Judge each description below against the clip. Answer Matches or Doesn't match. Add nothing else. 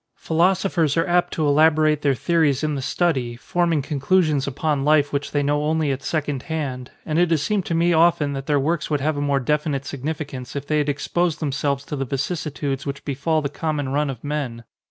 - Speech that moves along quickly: Matches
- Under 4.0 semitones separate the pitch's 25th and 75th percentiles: Matches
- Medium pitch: Matches